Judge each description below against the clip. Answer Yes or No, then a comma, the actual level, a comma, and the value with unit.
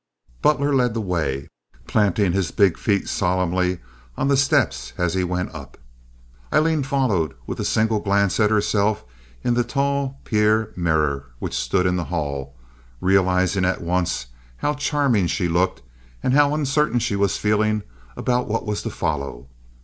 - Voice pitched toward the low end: Yes, low, 100 Hz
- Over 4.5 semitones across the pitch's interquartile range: Yes, wide, 5.6 semitones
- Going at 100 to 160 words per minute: Yes, average, 155 wpm